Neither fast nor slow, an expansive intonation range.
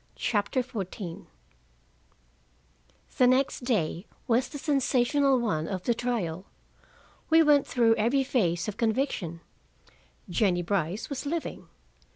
No: slow, 115 wpm; wide, 6.1 semitones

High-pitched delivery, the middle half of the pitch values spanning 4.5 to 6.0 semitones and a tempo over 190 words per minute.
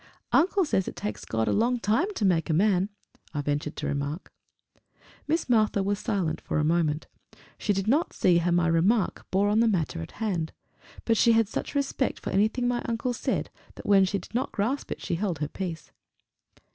Yes: high, 200 Hz; wide, 5.6 semitones; fast, 205 wpm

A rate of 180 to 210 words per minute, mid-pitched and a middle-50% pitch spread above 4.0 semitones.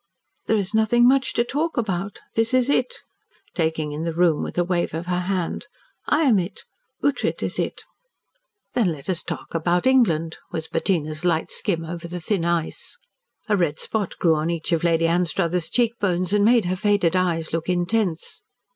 Yes: average, 190 wpm; medium, 180 Hz; average, 4.4 semitones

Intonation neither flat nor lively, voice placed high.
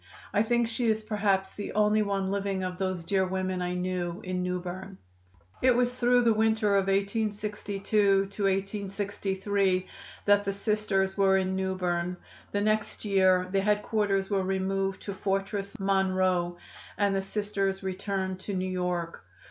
No: narrow, 1.7 semitones; high, 195 Hz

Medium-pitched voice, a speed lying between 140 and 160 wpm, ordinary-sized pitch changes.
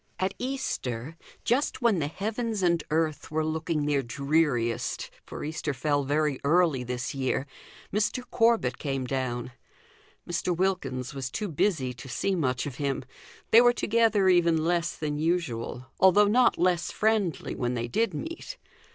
No: medium, 160 Hz; average, 150 wpm; wide, 6.3 semitones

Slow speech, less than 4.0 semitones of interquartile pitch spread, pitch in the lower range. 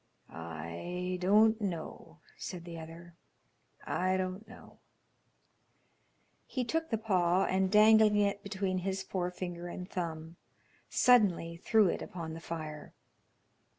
No: slow, 115 wpm; average, 3.3 semitones; medium, 185 Hz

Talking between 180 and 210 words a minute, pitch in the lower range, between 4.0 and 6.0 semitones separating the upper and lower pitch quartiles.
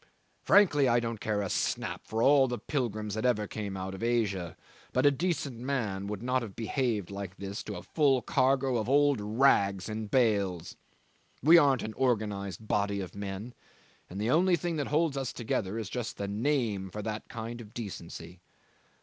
Yes: average, 185 wpm; low, 110 Hz; average, 4.6 semitones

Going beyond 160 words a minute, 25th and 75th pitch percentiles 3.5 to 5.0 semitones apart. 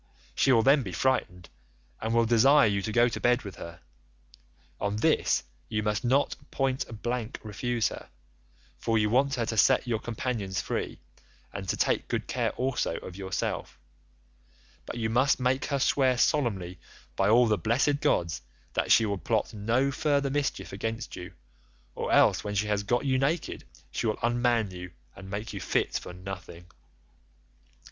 Yes: average, 170 wpm; average, 4.2 semitones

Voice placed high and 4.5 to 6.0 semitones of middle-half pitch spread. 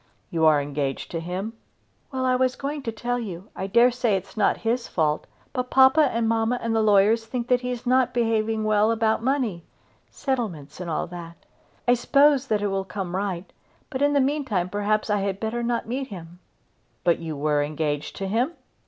Yes: high, 220 Hz; wide, 5.4 semitones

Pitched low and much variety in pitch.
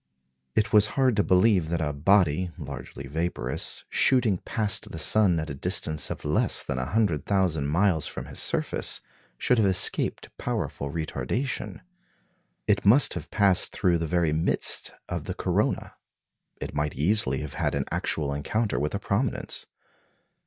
Yes: very low, 85 Hz; wide, 5.7 semitones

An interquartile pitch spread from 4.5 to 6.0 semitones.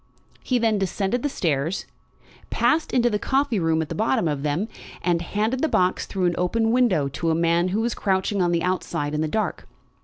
Yes: average, 5.2 semitones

